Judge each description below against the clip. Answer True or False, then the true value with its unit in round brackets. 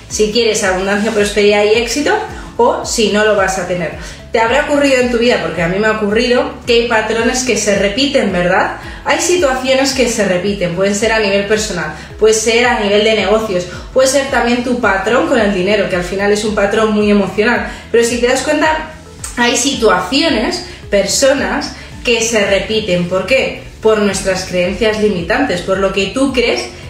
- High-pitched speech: True (220 Hz)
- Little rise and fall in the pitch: False (3.8 semitones)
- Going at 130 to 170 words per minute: False (190 wpm)